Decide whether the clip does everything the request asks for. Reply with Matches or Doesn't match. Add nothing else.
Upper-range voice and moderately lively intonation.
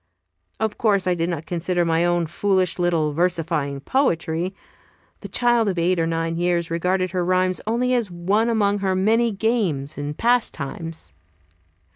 Doesn't match